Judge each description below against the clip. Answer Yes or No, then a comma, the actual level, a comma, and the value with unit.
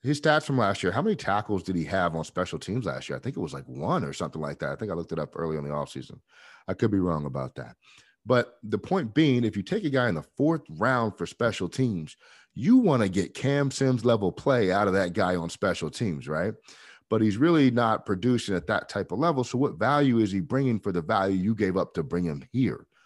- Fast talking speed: Yes, fast, 260 wpm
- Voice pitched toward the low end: Yes, low, 110 Hz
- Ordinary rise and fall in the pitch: No, wide, 6.2 semitones